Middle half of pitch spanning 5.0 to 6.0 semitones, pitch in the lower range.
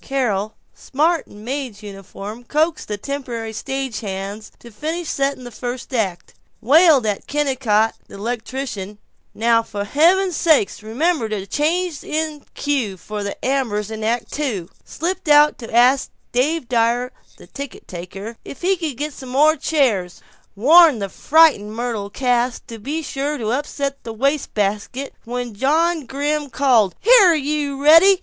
No: wide, 5.4 semitones; very high, 255 Hz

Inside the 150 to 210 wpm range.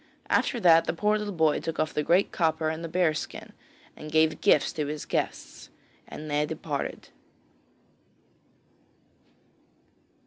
No: average, 140 wpm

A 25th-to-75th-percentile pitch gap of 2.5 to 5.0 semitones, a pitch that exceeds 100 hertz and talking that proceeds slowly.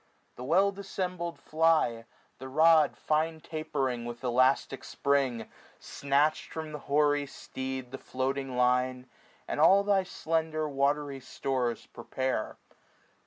Yes: average, 3.5 semitones; medium, 140 Hz; slow, 120 wpm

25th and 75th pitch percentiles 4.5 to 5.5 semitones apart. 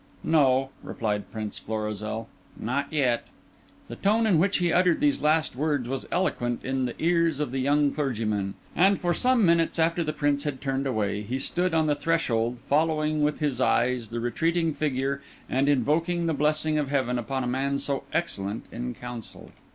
Yes: average, 4.8 semitones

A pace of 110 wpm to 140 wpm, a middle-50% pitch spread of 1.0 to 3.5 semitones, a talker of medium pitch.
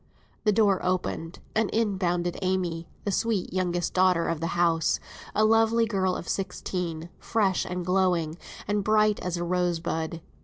No: average, 155 wpm; average, 2.9 semitones; medium, 180 Hz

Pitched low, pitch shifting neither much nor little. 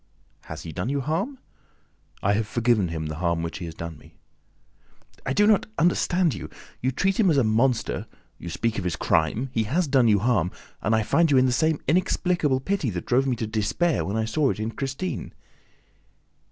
No: low, 120 Hz; wide, 7.3 semitones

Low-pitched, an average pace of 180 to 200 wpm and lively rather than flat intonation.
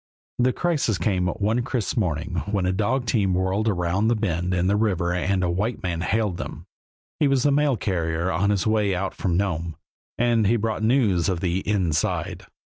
No: low, 100 Hz; average, 195 wpm; average, 3.9 semitones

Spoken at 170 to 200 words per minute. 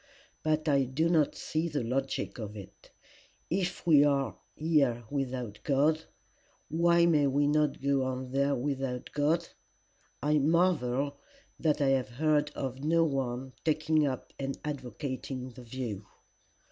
No: average, 140 wpm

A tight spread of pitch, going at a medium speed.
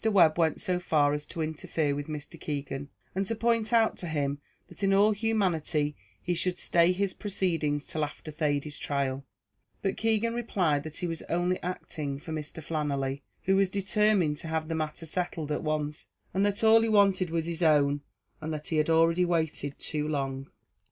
No: average, 4.3 semitones; average, 185 wpm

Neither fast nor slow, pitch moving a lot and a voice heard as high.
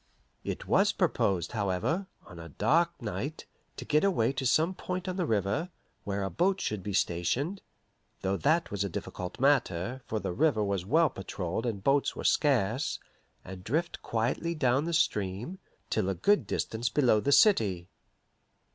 No: average, 165 wpm; wide, 8.4 semitones; low, 120 Hz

